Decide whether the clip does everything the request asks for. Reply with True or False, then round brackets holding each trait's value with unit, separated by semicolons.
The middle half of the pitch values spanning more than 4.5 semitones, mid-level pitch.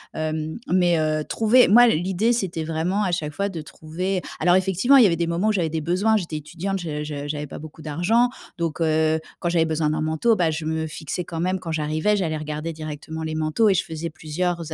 False (2.9 semitones; 165 Hz)